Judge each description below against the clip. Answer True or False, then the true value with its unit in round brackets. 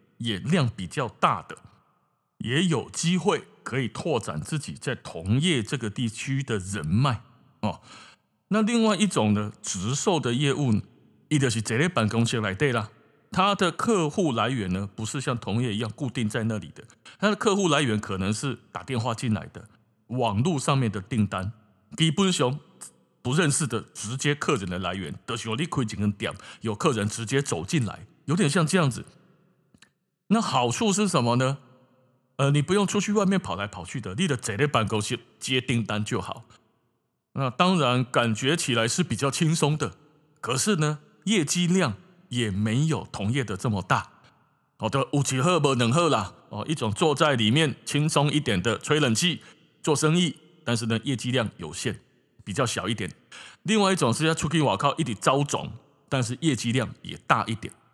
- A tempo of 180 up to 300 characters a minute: True (260 characters per minute)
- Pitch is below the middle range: True (130 Hz)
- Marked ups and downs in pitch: True (6.2 semitones)